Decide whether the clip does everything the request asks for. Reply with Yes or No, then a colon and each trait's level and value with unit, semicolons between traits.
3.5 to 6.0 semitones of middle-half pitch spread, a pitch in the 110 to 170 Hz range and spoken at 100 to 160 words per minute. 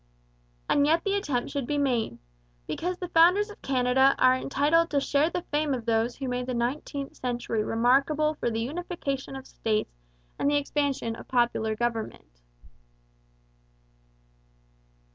No: average, 3.9 semitones; very high, 270 Hz; average, 145 wpm